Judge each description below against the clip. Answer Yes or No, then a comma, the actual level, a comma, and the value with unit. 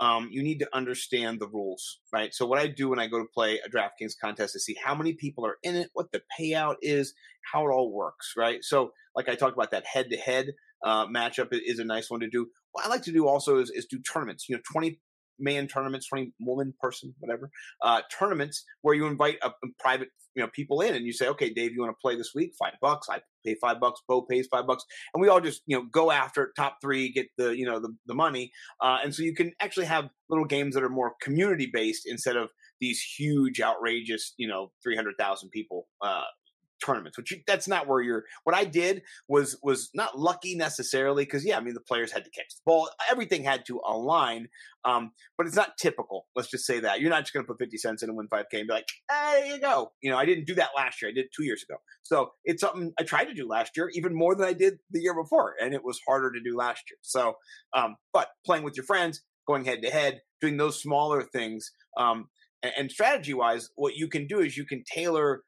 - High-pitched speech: No, medium, 140 Hz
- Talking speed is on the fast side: Yes, fast, 250 wpm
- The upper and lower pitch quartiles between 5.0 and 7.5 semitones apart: Yes, average, 5.3 semitones